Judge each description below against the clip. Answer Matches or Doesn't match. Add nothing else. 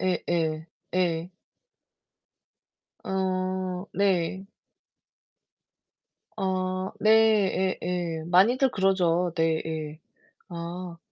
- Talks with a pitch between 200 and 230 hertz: Doesn't match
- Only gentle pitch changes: Matches